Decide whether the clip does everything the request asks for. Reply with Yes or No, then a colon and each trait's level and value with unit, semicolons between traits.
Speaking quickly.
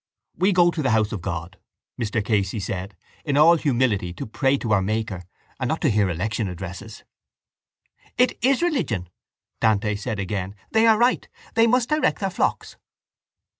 No: average, 170 wpm